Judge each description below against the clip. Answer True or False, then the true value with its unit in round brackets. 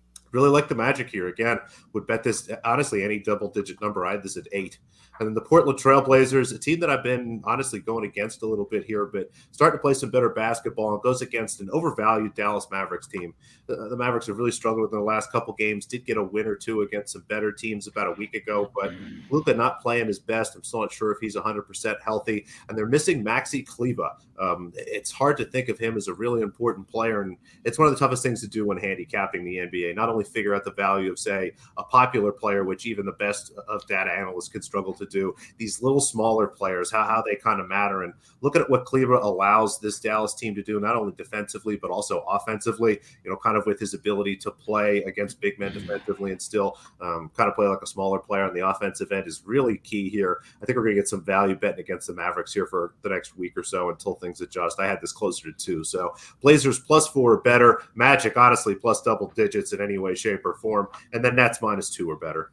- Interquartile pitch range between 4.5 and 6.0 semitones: False (3.4 semitones)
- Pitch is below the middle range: True (110 Hz)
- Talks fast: True (240 wpm)